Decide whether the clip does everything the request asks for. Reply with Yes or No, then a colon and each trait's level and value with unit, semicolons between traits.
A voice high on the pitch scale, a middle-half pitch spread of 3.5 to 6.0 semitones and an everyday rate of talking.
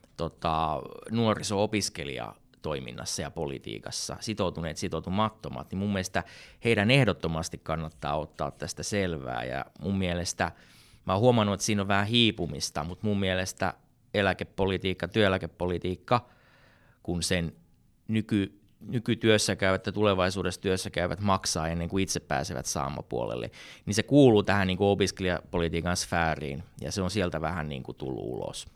No: very low, 95 Hz; average, 3.8 semitones; average, 130 wpm